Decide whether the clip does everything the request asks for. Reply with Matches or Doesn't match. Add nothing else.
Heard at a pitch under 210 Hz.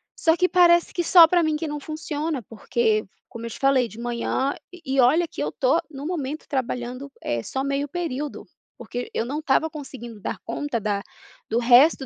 Doesn't match